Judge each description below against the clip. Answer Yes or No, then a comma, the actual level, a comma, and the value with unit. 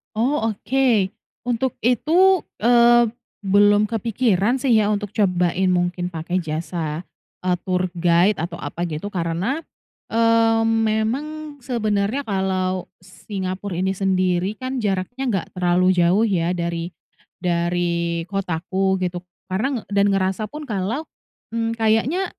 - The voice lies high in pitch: Yes, high, 195 Hz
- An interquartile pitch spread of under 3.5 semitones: No, average, 4.2 semitones